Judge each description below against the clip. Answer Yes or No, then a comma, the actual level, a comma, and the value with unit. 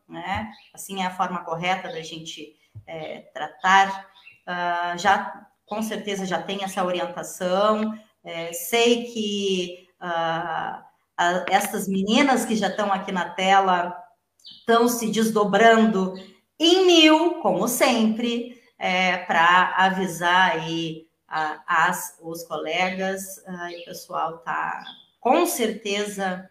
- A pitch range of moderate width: Yes, average, 3.7 semitones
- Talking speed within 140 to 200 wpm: No, slow, 120 wpm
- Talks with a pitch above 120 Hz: Yes, high, 190 Hz